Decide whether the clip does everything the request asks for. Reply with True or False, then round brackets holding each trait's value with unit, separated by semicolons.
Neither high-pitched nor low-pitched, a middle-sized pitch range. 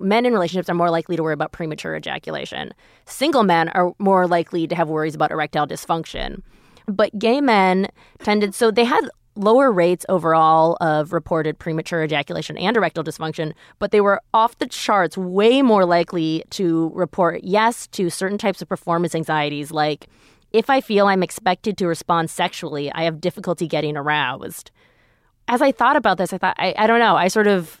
True (175 Hz; 4.0 semitones)